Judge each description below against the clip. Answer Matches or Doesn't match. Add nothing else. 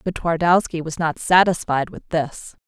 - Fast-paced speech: Doesn't match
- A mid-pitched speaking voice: Matches